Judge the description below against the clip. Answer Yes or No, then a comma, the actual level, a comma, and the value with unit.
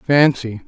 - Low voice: Yes, low, 125 Hz